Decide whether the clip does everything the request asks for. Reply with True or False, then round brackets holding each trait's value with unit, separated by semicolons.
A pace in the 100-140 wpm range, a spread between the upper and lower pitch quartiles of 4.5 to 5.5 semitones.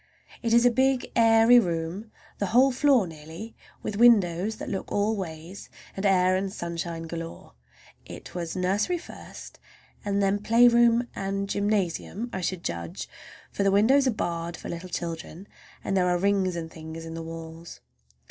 False (165 wpm; 4.9 semitones)